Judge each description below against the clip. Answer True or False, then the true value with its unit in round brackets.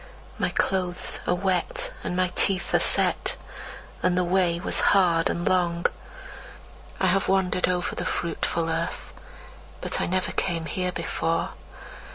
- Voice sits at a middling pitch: True (180 Hz)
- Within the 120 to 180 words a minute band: True (145 wpm)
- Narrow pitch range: True (1.5 semitones)